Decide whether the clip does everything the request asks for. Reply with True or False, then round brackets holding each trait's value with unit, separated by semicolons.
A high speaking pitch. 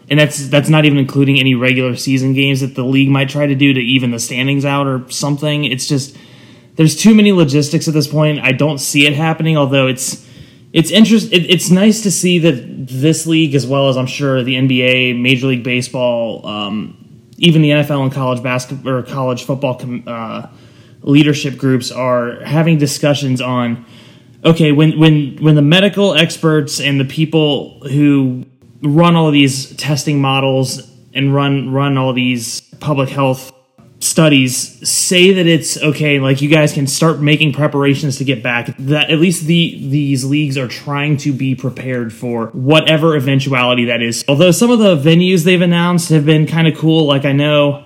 False (140 Hz)